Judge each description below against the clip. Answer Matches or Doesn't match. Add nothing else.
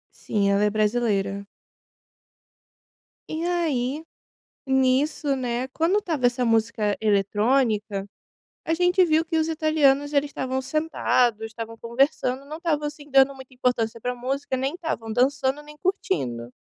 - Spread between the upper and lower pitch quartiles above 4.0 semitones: Matches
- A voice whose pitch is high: Matches